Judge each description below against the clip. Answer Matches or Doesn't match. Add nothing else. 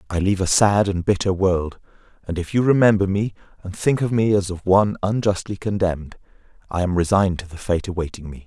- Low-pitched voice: Matches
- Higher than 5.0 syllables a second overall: Matches